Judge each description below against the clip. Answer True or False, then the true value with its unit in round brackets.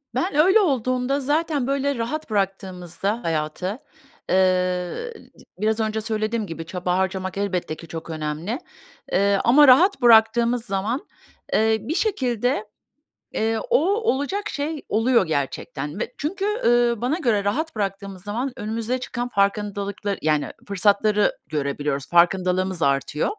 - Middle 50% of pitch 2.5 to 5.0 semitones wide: False (5.4 semitones)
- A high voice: True (215 Hz)